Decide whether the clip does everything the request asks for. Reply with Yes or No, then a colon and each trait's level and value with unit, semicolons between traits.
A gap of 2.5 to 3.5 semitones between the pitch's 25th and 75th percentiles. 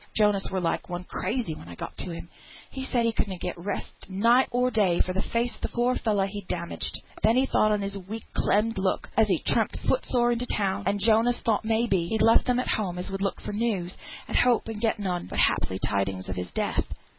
No: average, 4.0 semitones